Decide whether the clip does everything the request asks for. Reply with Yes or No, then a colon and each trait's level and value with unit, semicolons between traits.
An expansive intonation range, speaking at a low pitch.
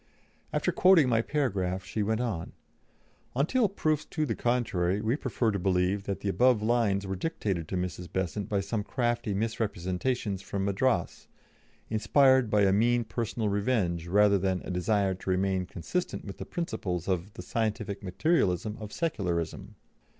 No: average, 4.1 semitones; low, 105 Hz